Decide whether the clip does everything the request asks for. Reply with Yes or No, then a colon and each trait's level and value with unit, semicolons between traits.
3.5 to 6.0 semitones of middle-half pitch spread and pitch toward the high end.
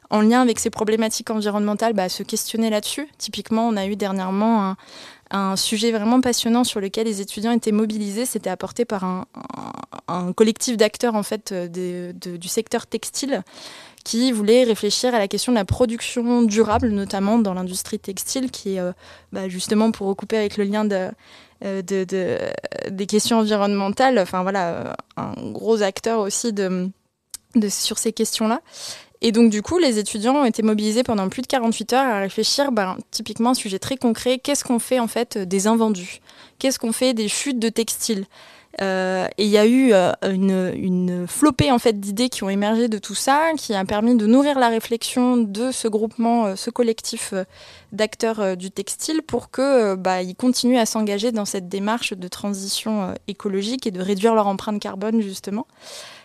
No: average, 3.1 semitones; high, 220 Hz